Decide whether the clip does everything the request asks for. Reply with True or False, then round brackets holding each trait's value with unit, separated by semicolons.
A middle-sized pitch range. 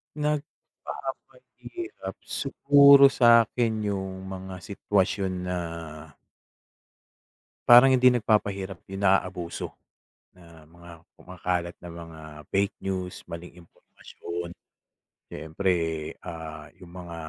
True (4.8 semitones)